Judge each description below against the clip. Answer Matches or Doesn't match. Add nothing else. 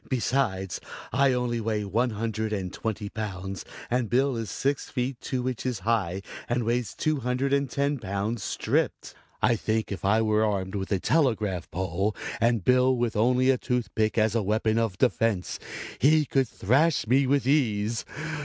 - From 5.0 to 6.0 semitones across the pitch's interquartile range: Doesn't match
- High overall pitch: Doesn't match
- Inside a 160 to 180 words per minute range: Matches